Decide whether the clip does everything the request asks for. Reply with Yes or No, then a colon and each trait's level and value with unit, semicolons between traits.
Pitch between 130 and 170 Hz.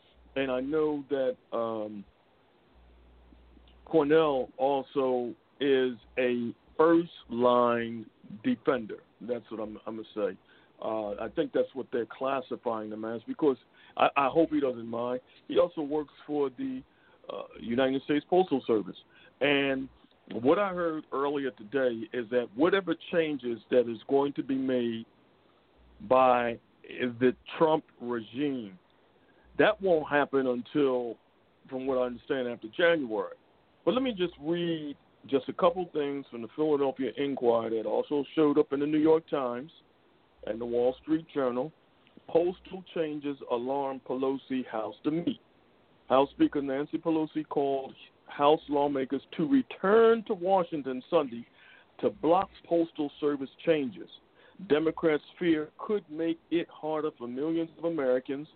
Yes: medium, 140 Hz